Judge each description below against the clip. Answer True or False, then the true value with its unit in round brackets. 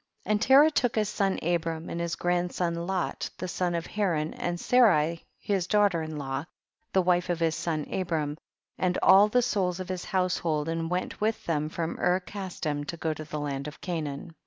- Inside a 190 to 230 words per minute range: True (195 wpm)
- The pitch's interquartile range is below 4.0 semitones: True (2.9 semitones)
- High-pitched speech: False (175 Hz)